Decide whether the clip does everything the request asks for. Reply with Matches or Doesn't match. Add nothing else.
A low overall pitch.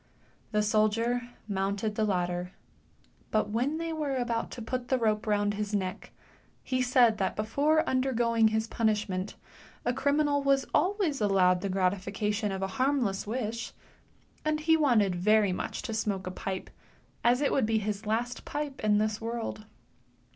Doesn't match